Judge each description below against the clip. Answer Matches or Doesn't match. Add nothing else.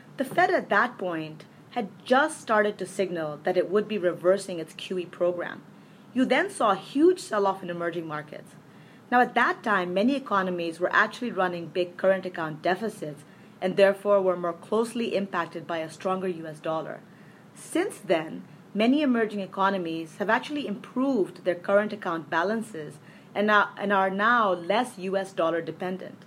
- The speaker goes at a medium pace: Matches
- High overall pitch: Matches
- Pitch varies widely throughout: Doesn't match